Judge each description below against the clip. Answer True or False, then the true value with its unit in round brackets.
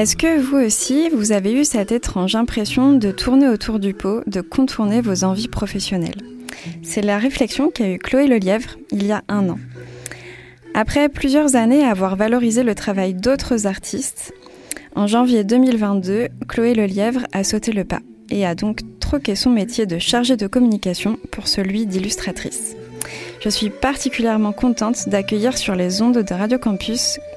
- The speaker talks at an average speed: True (165 wpm)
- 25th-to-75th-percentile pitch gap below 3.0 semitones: False (4.2 semitones)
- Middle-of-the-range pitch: False (215 Hz)